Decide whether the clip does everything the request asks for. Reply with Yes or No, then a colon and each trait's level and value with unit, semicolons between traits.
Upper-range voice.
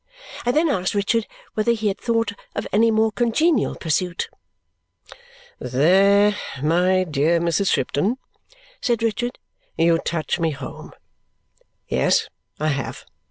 Yes: high, 195 Hz